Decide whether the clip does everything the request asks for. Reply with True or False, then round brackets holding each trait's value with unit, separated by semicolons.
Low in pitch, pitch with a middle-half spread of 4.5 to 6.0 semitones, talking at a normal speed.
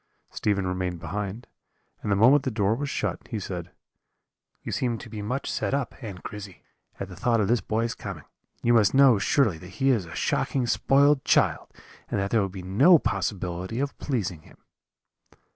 True (105 Hz; 5.0 semitones; 190 wpm)